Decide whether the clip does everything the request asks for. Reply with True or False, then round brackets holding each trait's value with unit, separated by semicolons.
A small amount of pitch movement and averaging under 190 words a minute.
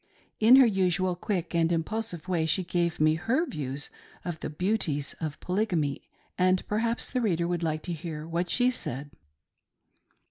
False (4.5 semitones; 165 wpm)